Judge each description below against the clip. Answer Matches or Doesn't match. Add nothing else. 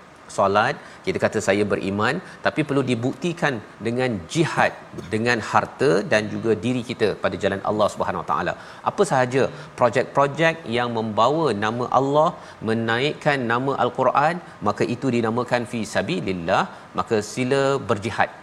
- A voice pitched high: Doesn't match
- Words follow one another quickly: Matches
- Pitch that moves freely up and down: Doesn't match